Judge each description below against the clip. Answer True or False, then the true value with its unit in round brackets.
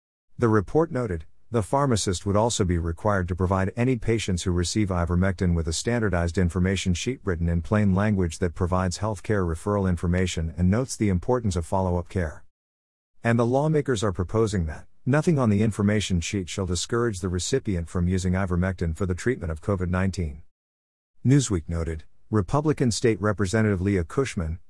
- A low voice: True (95 Hz)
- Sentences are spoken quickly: False (170 wpm)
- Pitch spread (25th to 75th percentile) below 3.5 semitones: False (3.8 semitones)